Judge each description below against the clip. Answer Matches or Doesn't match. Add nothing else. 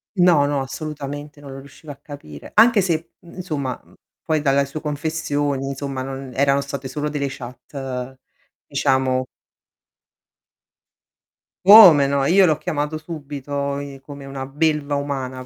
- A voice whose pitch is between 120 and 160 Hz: Matches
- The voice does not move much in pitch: Matches